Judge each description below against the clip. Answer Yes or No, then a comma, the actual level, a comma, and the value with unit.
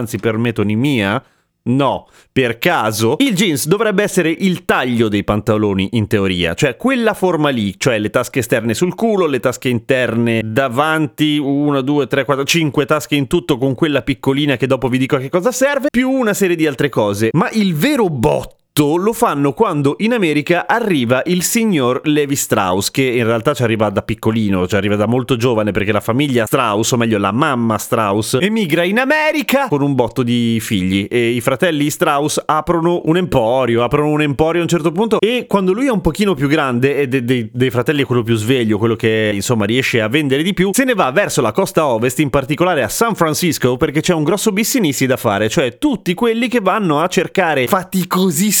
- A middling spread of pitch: No, wide, 7.1 semitones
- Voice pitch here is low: No, medium, 145 Hz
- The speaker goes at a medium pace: No, fast, 200 wpm